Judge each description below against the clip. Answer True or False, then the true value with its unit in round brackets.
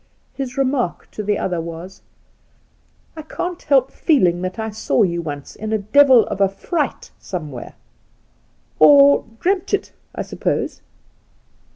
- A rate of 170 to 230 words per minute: False (135 wpm)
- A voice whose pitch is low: False (210 Hz)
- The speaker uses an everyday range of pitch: False (8.0 semitones)